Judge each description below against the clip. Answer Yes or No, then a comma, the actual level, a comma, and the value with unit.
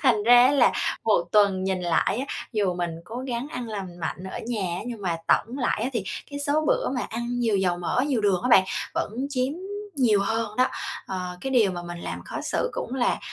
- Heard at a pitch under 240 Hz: Yes, high, 220 Hz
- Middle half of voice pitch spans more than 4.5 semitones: Yes, average, 5.0 semitones